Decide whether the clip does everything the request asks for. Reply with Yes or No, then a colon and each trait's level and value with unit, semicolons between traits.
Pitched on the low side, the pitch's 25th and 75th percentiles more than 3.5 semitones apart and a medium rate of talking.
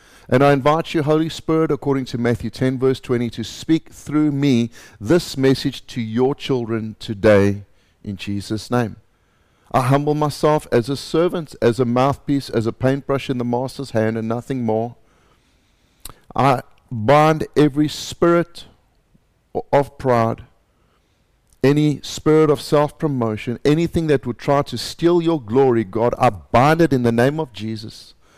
Yes: low, 130 Hz; average, 4.4 semitones; average, 150 wpm